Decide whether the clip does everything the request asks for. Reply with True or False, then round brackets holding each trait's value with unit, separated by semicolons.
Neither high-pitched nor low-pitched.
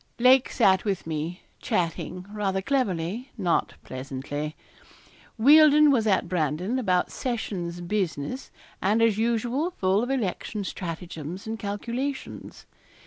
False (200 Hz)